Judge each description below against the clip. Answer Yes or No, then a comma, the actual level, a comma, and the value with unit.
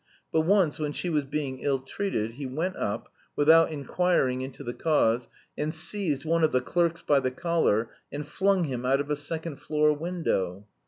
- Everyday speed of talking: Yes, average, 190 wpm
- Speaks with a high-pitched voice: No, medium, 150 Hz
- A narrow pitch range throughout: No, average, 4.1 semitones